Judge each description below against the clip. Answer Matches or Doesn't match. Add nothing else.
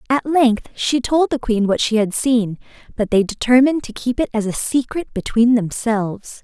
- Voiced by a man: Doesn't match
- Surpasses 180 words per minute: Matches